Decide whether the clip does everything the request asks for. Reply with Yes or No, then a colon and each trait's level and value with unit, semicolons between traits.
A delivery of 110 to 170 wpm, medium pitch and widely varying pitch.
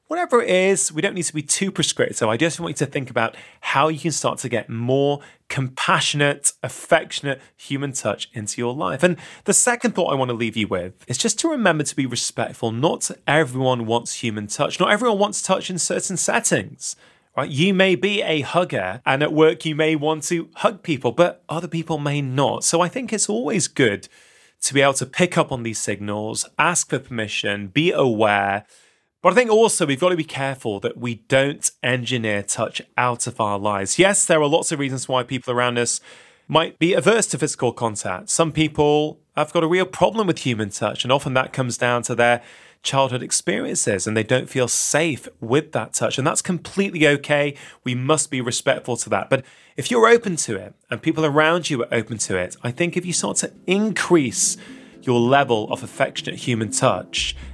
No: fast, 205 wpm; medium, 145 Hz; wide, 6.1 semitones